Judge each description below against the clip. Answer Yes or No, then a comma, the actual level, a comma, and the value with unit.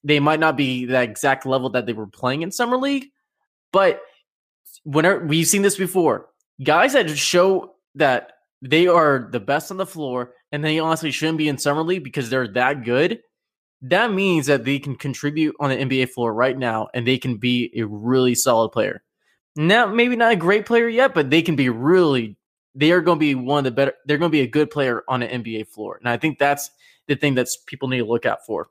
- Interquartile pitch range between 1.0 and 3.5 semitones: No, average, 4.5 semitones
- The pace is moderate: No, fast, 225 wpm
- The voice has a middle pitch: Yes, medium, 145 Hz